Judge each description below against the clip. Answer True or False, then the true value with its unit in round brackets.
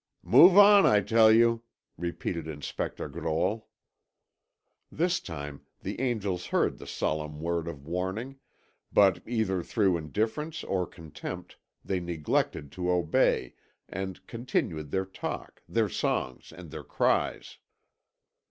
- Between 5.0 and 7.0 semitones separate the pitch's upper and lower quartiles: True (5.5 semitones)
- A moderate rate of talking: False (120 wpm)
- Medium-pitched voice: False (95 Hz)